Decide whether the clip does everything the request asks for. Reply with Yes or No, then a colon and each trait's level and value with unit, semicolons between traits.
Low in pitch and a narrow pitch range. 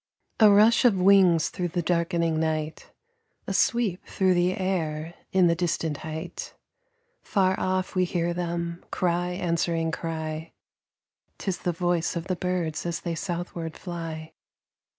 No: medium, 175 Hz; narrow, 1.9 semitones